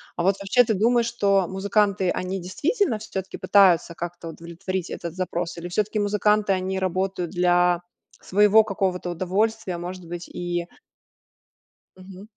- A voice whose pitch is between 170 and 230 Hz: Yes, high, 190 Hz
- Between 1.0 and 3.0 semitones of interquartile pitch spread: Yes, average, 2.7 semitones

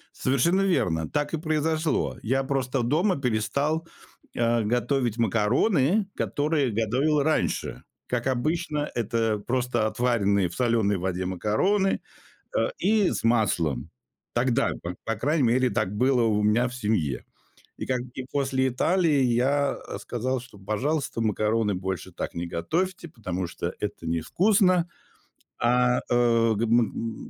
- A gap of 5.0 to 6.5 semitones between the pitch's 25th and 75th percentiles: Yes, wide, 5.4 semitones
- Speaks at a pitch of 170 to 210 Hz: No, low, 125 Hz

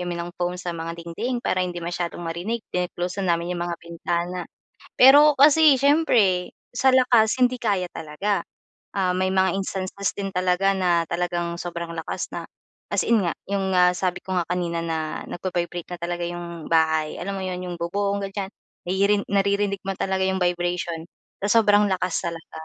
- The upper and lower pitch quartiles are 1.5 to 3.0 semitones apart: Yes, narrow, 2.5 semitones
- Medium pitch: Yes, medium, 180 Hz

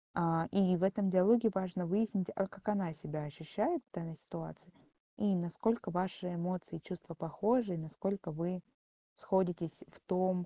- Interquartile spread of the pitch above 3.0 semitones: No, average, 2.7 semitones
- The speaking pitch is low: No, medium, 185 Hz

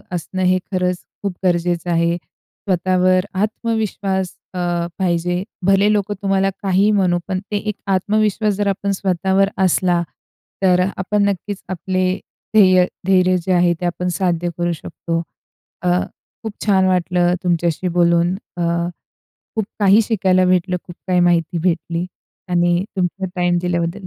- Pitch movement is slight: Yes, narrow, 1.9 semitones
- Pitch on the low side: No, medium, 185 Hz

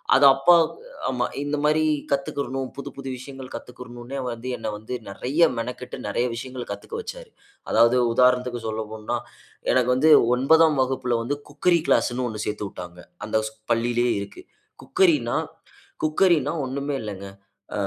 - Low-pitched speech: Yes, low, 130 Hz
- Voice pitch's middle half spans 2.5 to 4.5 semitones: Yes, average, 3.4 semitones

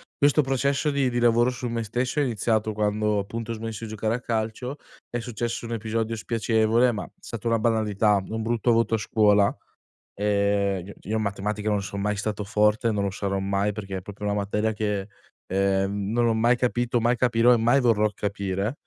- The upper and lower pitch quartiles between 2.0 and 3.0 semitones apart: Yes, narrow, 2.4 semitones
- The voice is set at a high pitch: No, low, 110 Hz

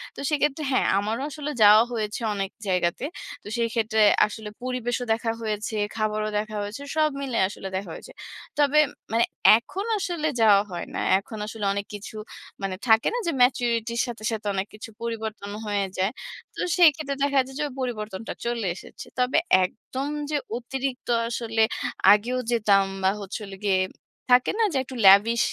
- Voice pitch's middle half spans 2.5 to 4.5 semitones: Yes, average, 3.5 semitones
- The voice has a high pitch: Yes, high, 225 Hz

